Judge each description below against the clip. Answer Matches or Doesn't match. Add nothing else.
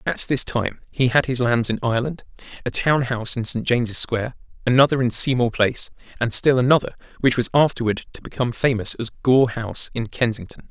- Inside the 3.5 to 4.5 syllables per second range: Doesn't match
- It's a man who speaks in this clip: Matches